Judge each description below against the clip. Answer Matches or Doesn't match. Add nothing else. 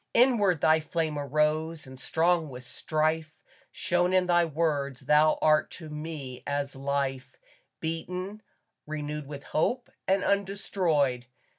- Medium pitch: Matches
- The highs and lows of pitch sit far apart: Doesn't match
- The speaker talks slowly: Matches